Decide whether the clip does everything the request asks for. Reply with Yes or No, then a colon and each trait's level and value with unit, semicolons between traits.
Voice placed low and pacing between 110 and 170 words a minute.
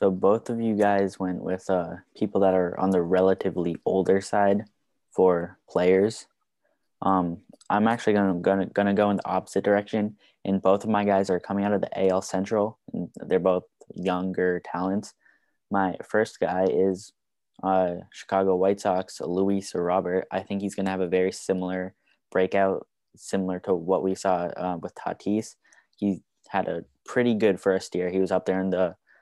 No: very low, 95 Hz; average, 180 wpm